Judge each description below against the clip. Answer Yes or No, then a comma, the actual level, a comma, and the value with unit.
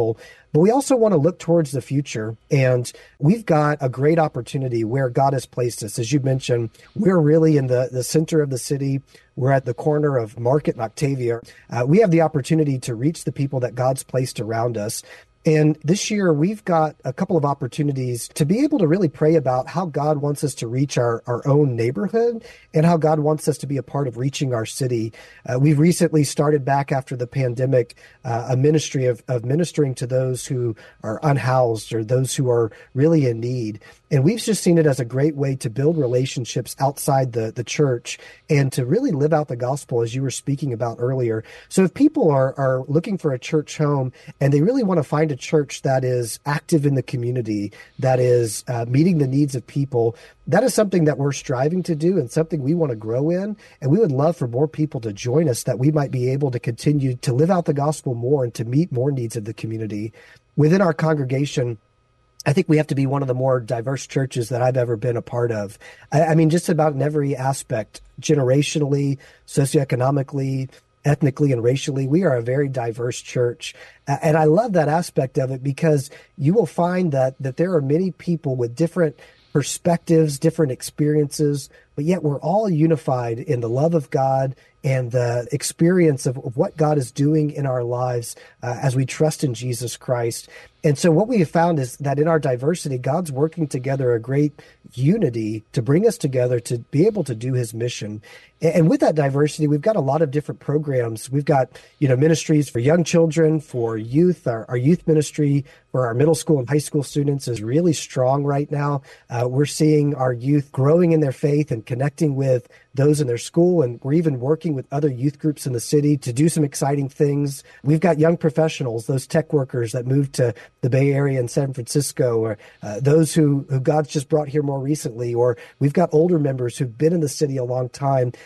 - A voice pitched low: No, medium, 145 Hz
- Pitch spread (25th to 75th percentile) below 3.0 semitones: No, average, 4.0 semitones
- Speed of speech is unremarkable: No, fast, 210 wpm